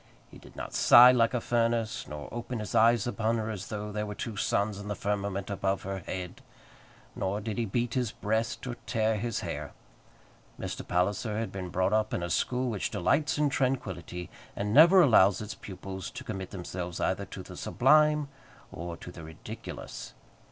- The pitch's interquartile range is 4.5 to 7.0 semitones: No, average, 3.7 semitones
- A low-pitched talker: Yes, low, 105 Hz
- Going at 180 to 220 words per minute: Yes, average, 185 wpm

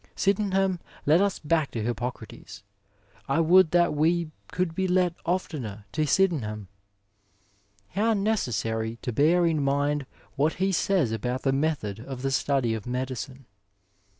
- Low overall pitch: No, medium, 150 Hz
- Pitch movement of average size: No, wide, 6.3 semitones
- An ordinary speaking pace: Yes, average, 150 wpm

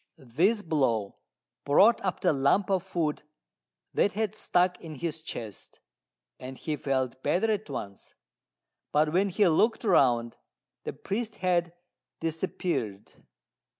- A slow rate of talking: Yes, slow, 125 wpm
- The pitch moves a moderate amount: No, wide, 6.3 semitones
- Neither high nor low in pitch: Yes, medium, 165 Hz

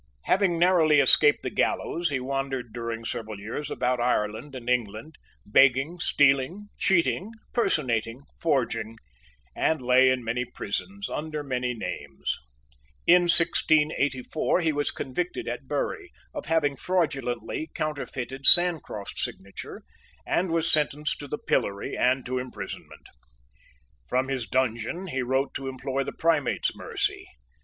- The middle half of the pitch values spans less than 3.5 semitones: No, average, 4.5 semitones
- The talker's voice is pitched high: No, low, 135 Hz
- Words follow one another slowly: Yes, slow, 130 wpm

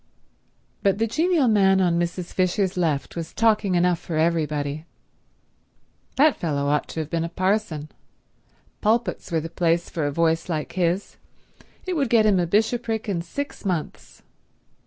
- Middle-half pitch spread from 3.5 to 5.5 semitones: Yes, average, 4.6 semitones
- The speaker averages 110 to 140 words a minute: No, average, 155 wpm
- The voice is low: No, medium, 180 Hz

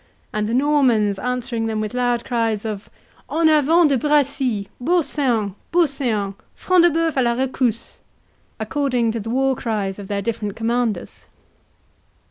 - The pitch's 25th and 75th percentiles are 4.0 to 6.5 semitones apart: Yes, average, 4.5 semitones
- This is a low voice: No, high, 245 Hz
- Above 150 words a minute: No, average, 145 wpm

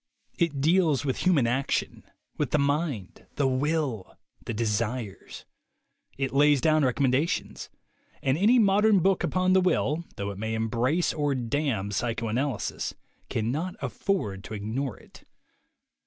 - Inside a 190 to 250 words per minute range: No, average, 140 wpm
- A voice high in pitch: No, low, 135 Hz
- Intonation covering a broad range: Yes, wide, 5.7 semitones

